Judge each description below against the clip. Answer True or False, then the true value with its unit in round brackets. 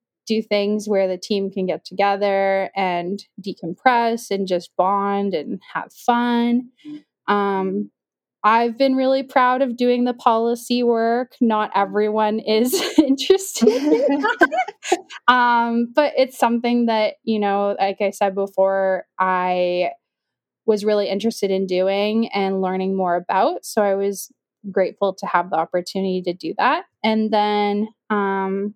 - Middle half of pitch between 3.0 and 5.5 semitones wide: True (3.7 semitones)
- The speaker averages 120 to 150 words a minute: True (135 wpm)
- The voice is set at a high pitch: True (210 Hz)